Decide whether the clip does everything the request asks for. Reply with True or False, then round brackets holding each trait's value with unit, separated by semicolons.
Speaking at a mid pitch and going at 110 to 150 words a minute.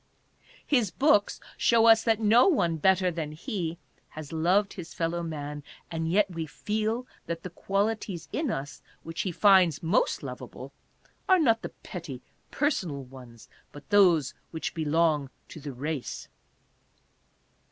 True (170 Hz; 140 wpm)